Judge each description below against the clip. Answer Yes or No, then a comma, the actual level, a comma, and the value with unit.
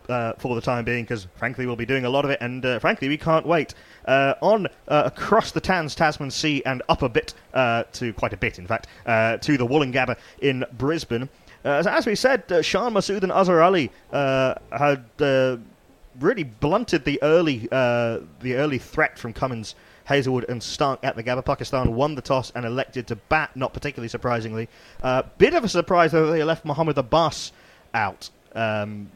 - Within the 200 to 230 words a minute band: Yes, fast, 205 wpm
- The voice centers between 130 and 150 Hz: Yes, low, 135 Hz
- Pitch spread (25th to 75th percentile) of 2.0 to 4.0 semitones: No, average, 4.5 semitones